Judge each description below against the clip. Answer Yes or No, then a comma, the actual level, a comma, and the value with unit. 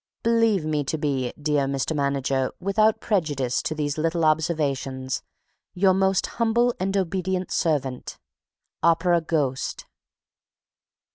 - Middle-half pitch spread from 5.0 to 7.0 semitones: Yes, average, 5.3 semitones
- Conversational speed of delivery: No, slow, 115 wpm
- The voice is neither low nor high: Yes, medium, 160 Hz